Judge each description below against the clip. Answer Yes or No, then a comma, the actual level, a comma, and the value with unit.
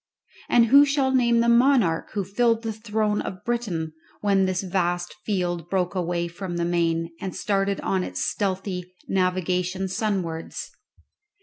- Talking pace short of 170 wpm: Yes, average, 145 wpm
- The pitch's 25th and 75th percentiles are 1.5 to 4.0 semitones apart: Yes, average, 3.7 semitones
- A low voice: No, high, 190 Hz